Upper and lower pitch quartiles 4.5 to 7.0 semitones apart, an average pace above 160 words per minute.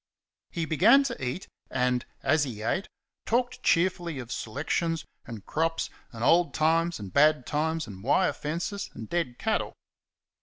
No: wide, 5.5 semitones; average, 150 wpm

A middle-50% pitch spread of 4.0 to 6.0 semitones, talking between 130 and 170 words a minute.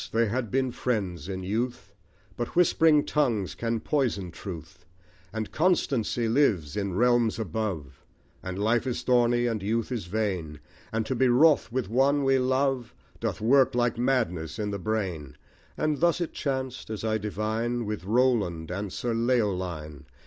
Yes: average, 4.6 semitones; average, 155 wpm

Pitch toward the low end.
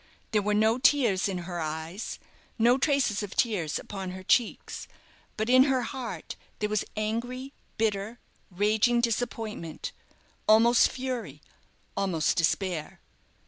No: high, 215 Hz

